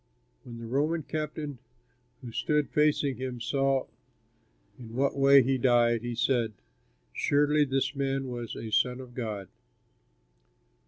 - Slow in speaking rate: Yes, slow, 130 wpm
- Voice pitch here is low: Yes, low, 130 Hz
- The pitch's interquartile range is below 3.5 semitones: Yes, average, 2.8 semitones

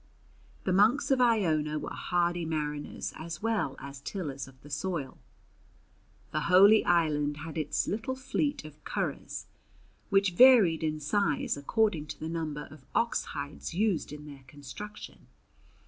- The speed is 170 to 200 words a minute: No, average, 145 wpm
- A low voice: No, medium, 160 Hz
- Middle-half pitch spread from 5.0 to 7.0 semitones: Yes, wide, 5.6 semitones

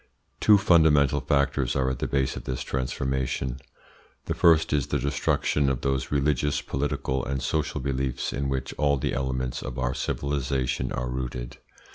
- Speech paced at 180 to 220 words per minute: No, average, 160 wpm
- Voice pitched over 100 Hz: No, very low, 65 Hz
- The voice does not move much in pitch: Yes, narrow, 1.8 semitones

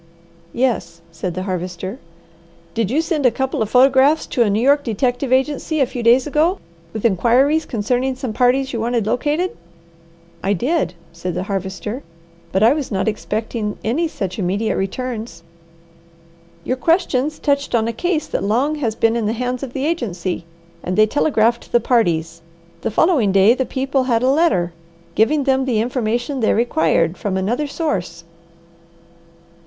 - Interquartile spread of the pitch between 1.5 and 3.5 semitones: No, average, 5.0 semitones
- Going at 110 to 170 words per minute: Yes, average, 165 wpm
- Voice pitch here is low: No, high, 235 Hz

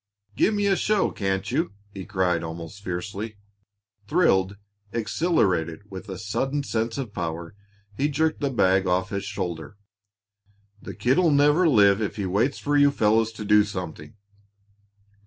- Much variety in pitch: Yes, wide, 6.9 semitones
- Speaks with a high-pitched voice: No, low, 105 Hz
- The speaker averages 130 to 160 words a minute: Yes, average, 150 wpm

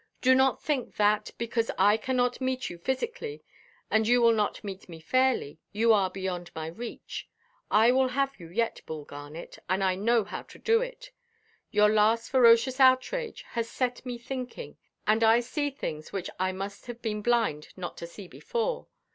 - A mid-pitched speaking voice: No, high, 230 Hz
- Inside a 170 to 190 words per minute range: Yes, average, 180 wpm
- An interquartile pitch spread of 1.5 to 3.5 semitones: No, average, 4.9 semitones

